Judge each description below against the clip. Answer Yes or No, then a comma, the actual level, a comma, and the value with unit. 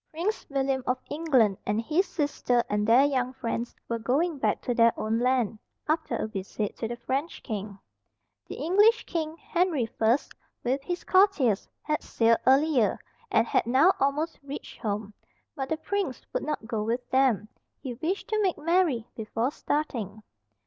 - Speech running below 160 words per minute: No, average, 165 wpm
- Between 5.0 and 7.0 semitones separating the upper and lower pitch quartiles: Yes, wide, 5.6 semitones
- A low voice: No, very high, 265 Hz